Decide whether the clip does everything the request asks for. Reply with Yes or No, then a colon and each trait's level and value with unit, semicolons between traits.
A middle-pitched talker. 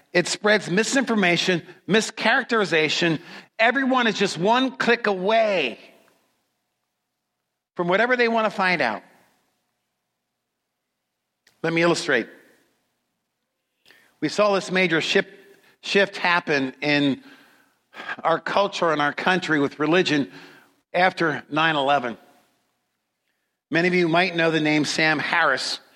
Yes: medium, 180 Hz